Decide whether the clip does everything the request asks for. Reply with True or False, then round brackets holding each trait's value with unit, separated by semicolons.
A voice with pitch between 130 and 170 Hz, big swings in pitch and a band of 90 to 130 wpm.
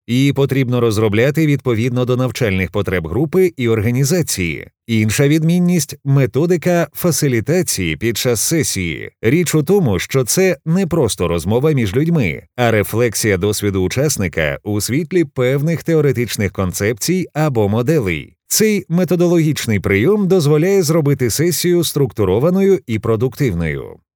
True (135 Hz; 7.1 semitones; 115 wpm)